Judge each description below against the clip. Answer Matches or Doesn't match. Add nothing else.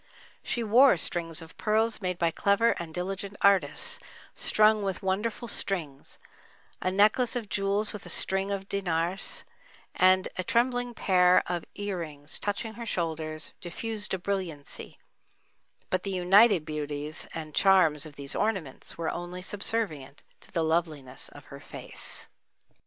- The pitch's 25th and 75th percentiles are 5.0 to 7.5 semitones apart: Doesn't match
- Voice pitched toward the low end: Doesn't match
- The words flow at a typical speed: Matches